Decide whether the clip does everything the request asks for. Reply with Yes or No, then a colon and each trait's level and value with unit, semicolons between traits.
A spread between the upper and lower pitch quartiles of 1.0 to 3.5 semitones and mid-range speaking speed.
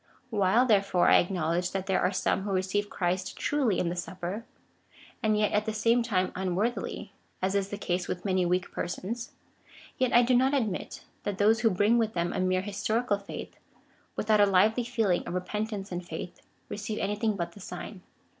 Yes: average, 3.1 semitones; average, 195 wpm